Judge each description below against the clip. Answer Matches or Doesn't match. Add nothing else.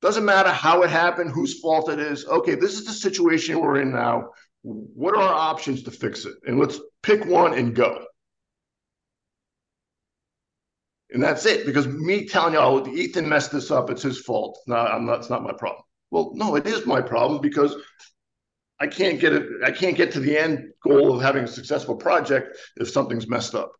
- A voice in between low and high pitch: Matches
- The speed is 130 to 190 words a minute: Doesn't match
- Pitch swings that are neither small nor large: Matches